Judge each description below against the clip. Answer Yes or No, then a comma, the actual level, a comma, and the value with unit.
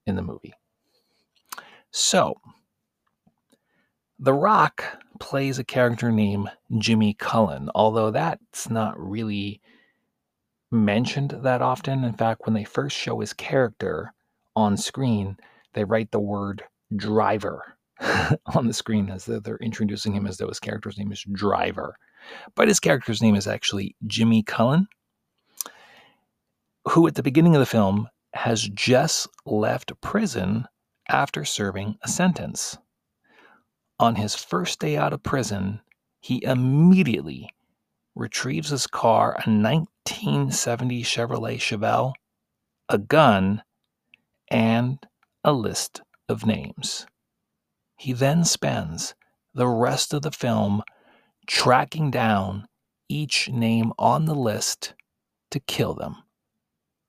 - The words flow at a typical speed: No, slow, 120 wpm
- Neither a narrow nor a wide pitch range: Yes, average, 3.6 semitones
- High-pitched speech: No, low, 115 Hz